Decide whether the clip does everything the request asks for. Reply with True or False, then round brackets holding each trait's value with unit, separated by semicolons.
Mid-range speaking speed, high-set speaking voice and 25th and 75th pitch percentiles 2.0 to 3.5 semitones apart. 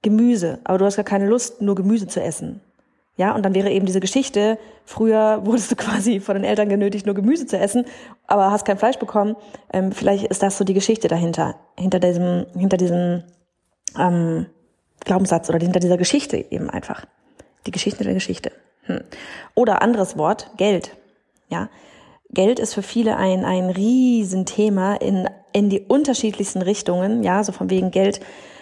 True (170 wpm; 200 Hz; 2.9 semitones)